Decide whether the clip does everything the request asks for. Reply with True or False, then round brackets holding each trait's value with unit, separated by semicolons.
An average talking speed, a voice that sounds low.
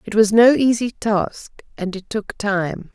False (185 wpm; 215 Hz)